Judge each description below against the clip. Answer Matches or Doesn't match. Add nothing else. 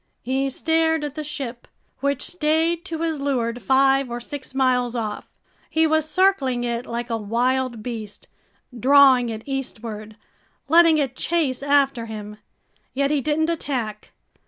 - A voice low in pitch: Doesn't match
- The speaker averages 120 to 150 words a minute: Matches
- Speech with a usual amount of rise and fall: Matches